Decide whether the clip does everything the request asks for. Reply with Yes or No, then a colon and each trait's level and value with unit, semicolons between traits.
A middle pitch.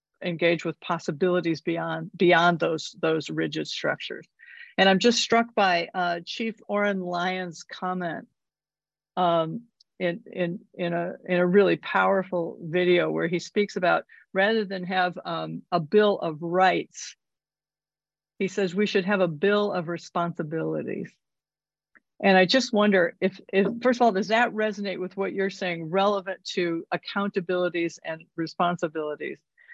Yes: medium, 180 Hz